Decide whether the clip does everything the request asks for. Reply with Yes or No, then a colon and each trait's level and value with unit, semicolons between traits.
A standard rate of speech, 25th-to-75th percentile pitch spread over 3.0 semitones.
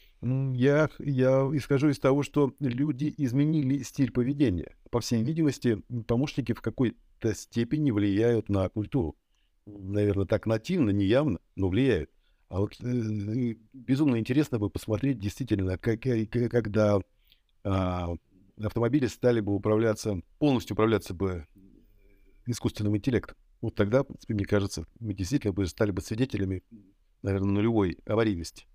Yes: average, 130 wpm; average, 4.7 semitones